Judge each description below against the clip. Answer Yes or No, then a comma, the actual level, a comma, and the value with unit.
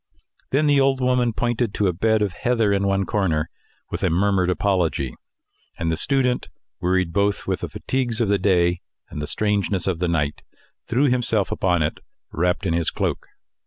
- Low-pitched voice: Yes, low, 100 Hz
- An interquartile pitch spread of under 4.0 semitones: No, average, 5.2 semitones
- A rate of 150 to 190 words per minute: Yes, average, 185 wpm